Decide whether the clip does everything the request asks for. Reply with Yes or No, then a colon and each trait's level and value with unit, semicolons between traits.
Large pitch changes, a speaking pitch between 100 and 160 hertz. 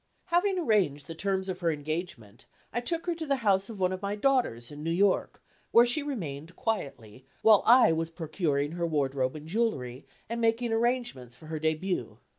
No: wide, 7.6 semitones; medium, 185 Hz